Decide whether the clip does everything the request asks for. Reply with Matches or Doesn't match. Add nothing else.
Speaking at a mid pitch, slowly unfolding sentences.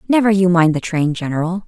Doesn't match